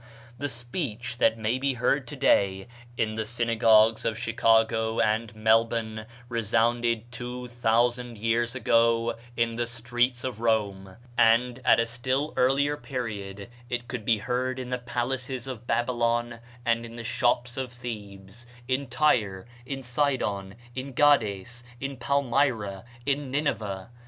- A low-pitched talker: Yes, low, 120 Hz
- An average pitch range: No, narrow, 2.0 semitones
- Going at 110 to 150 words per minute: Yes, slow, 135 wpm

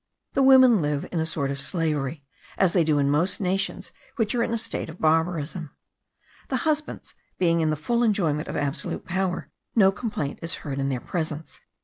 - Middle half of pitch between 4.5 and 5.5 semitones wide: Yes, average, 5.1 semitones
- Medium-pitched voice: Yes, medium, 165 Hz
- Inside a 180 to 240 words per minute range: Yes, average, 195 wpm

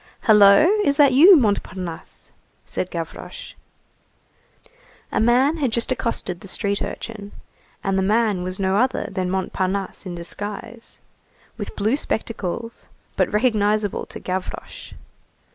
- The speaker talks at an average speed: No, slow, 125 wpm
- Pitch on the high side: Yes, high, 205 Hz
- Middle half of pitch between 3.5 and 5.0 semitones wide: Yes, average, 3.8 semitones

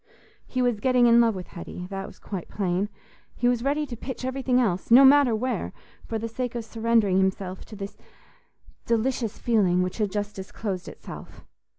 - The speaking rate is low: No, average, 170 wpm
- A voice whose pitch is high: Yes, high, 225 Hz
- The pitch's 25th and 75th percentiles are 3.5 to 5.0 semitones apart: Yes, average, 4.2 semitones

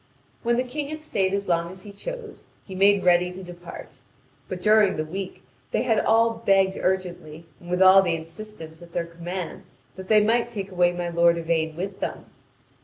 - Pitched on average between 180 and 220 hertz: Yes, medium, 185 Hz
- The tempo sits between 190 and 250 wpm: Yes, average, 195 wpm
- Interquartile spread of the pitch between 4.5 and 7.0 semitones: No, average, 3.4 semitones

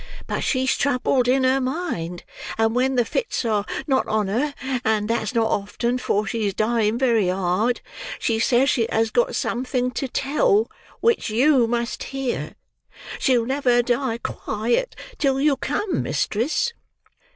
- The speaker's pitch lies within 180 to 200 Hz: No, high, 245 Hz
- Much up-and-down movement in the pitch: No, average, 3.3 semitones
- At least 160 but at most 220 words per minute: No, average, 145 wpm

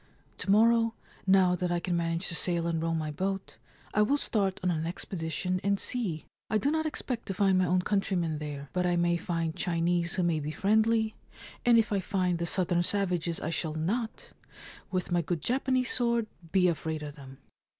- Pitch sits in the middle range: Yes, medium, 180 Hz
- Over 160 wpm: Yes, average, 200 wpm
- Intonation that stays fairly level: No, average, 3.5 semitones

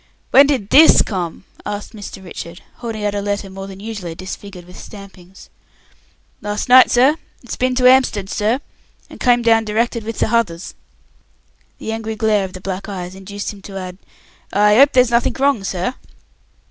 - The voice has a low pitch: No, high, 210 Hz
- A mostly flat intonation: No, average, 3.5 semitones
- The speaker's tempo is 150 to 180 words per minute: Yes, average, 175 wpm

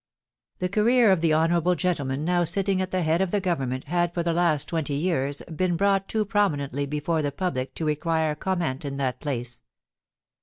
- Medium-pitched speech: Yes, medium, 165 Hz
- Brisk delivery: No, average, 190 wpm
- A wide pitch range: No, average, 4.2 semitones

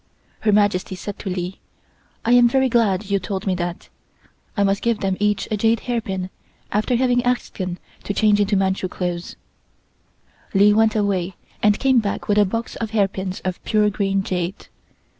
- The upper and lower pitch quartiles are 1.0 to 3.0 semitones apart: Yes, narrow, 2.6 semitones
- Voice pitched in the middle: No, high, 205 Hz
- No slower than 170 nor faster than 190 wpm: Yes, average, 180 wpm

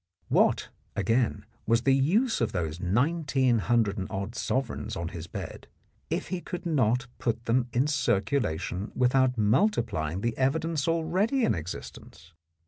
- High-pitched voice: No, low, 120 Hz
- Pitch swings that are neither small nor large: No, wide, 6.3 semitones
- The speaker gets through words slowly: No, average, 145 wpm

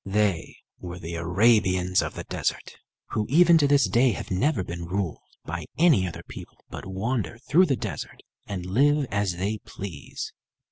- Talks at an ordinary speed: Yes, average, 170 wpm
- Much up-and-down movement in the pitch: Yes, wide, 6.5 semitones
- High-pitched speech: No, low, 100 Hz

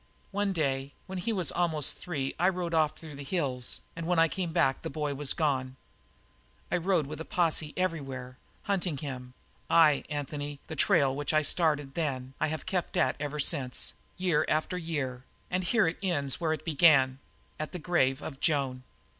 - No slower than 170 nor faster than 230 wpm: Yes, average, 185 wpm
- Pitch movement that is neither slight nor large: Yes, average, 4.1 semitones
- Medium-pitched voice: Yes, medium, 155 Hz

